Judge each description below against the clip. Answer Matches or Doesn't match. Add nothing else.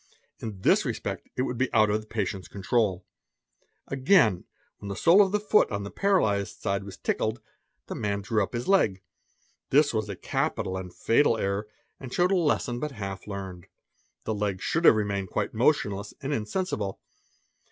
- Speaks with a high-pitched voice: Doesn't match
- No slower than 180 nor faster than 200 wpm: Matches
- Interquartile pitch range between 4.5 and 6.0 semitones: Matches